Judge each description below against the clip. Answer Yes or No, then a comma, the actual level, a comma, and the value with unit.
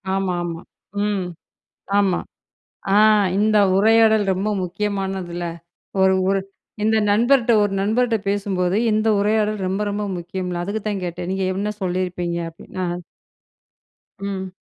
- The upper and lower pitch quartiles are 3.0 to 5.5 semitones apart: No, narrow, 2.6 semitones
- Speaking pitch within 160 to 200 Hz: Yes, high, 195 Hz